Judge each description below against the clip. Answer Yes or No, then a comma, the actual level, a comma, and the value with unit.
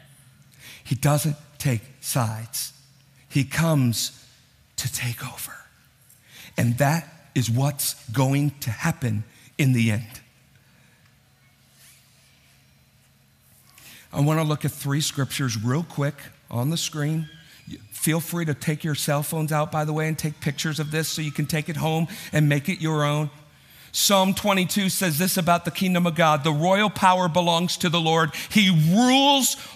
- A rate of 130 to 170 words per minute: Yes, average, 155 wpm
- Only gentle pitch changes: No, average, 3.6 semitones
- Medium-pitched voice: Yes, medium, 150 Hz